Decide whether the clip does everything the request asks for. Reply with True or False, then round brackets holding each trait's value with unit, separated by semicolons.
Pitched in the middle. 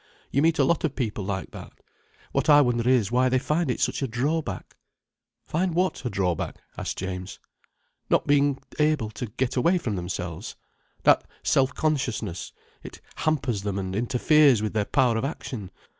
False (125 Hz)